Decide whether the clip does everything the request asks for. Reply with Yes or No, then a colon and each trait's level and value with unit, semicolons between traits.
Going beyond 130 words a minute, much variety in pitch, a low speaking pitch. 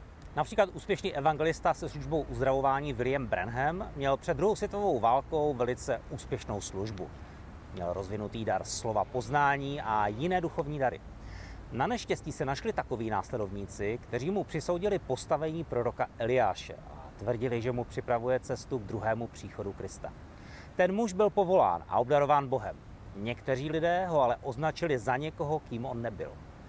Yes: average, 145 wpm; wide, 6.1 semitones; low, 130 Hz